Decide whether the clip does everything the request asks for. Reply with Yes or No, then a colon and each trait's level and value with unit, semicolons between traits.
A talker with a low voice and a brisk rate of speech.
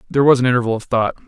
Yes: low, 125 Hz; fast, 285 wpm